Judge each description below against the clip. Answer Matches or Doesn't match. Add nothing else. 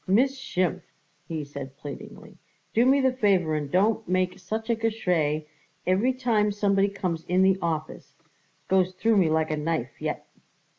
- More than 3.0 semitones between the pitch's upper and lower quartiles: Matches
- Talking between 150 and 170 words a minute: Matches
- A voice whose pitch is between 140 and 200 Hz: Matches